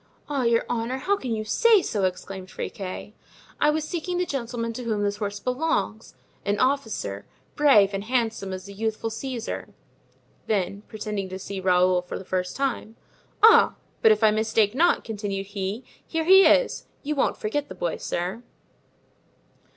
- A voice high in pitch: Yes, high, 220 Hz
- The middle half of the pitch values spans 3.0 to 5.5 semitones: Yes, average, 5.1 semitones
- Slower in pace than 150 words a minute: No, average, 165 wpm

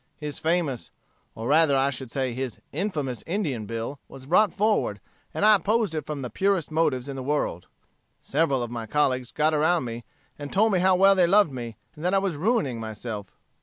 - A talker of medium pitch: Yes, medium, 150 Hz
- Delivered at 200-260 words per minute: Yes, fast, 205 wpm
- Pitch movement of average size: No, wide, 6.2 semitones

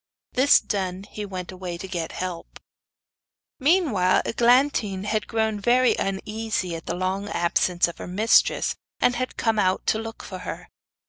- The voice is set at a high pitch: Yes, high, 200 Hz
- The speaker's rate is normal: Yes, average, 155 wpm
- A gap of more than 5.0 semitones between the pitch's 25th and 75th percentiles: No, average, 3.6 semitones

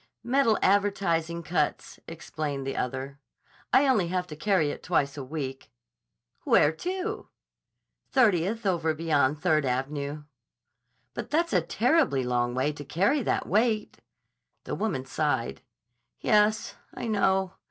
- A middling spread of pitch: No, wide, 6.7 semitones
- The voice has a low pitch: No, medium, 165 Hz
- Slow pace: Yes, slow, 130 wpm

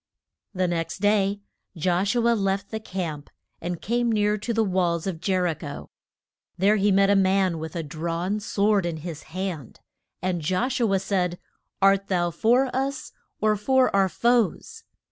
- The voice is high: Yes, high, 195 Hz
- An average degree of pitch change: Yes, average, 3.5 semitones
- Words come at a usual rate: Yes, average, 175 wpm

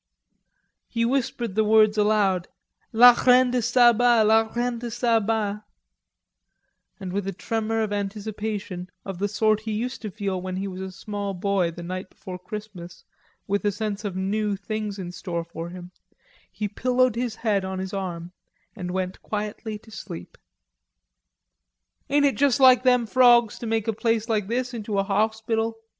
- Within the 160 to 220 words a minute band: Yes, average, 170 wpm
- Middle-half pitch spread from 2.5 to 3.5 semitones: Yes, average, 3.0 semitones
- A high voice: Yes, high, 215 Hz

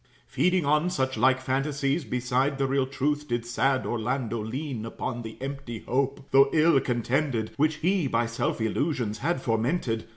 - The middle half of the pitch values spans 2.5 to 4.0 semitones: Yes, average, 3.3 semitones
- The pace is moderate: Yes, average, 160 wpm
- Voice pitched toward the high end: No, low, 130 Hz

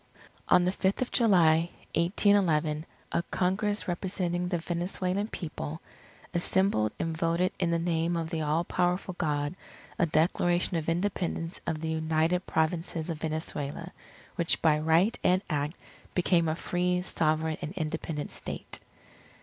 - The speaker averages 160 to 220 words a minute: No, average, 140 wpm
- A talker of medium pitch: Yes, medium, 170 Hz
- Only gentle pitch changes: Yes, narrow, 2.2 semitones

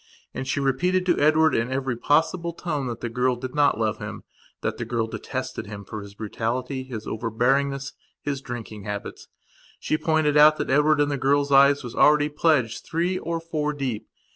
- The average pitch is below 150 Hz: Yes, low, 135 Hz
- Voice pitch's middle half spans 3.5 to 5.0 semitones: Yes, average, 4.1 semitones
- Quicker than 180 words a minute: Yes, average, 190 wpm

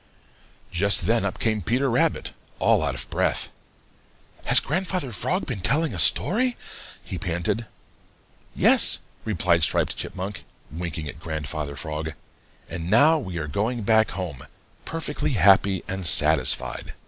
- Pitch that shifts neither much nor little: No, wide, 6.2 semitones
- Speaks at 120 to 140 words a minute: Yes, slow, 135 wpm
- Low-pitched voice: Yes, very low, 95 Hz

